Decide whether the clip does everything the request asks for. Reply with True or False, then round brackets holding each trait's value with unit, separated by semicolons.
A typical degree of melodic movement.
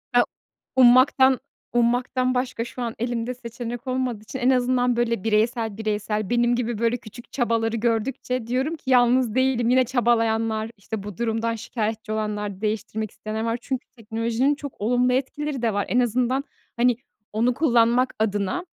False (2.2 semitones)